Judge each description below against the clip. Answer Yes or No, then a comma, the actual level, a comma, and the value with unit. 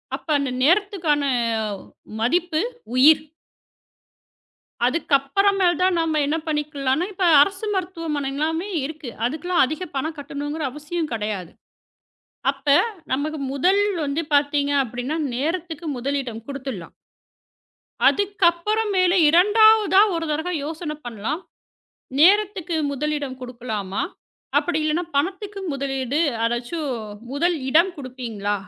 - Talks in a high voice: Yes, very high, 305 Hz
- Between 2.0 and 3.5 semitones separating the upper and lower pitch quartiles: No, average, 4.5 semitones